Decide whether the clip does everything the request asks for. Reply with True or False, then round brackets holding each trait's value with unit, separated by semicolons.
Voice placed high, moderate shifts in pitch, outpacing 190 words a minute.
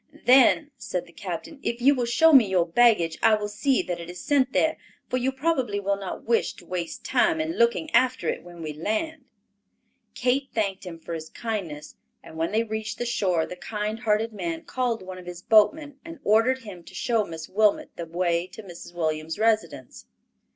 False (215 Hz; 6.3 semitones; 200 wpm)